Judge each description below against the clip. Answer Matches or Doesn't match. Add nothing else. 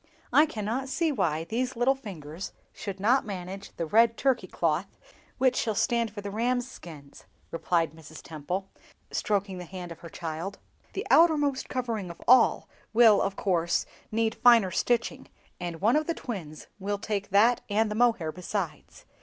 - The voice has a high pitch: Matches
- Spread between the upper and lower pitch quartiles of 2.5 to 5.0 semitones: Doesn't match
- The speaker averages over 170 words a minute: Doesn't match